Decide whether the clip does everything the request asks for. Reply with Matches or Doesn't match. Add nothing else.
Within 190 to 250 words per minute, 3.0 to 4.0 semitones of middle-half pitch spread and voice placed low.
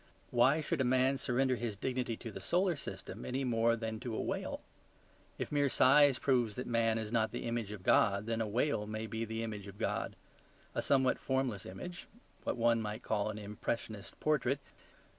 Matches